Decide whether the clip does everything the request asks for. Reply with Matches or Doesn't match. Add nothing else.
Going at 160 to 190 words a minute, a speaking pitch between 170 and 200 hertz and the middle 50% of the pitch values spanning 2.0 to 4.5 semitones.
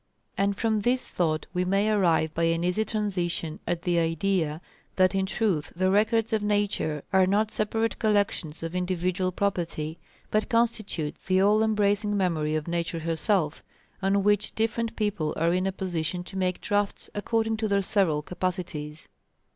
Matches